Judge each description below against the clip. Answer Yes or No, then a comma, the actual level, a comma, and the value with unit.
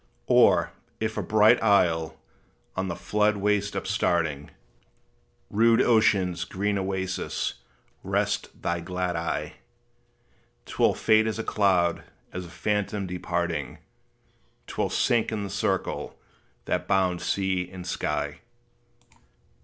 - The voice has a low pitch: Yes, very low, 95 Hz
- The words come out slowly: Yes, slow, 120 wpm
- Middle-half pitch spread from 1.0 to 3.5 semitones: Yes, average, 3.0 semitones